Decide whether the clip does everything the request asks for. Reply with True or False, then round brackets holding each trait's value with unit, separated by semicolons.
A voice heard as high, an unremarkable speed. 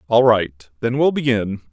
False (110 Hz; 175 wpm)